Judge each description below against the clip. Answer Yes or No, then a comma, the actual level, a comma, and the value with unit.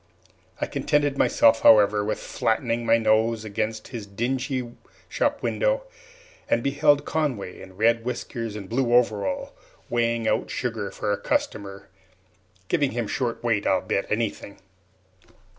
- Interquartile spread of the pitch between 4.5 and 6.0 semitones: No, average, 2.9 semitones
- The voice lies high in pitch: No, low, 115 Hz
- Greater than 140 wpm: No, slow, 135 wpm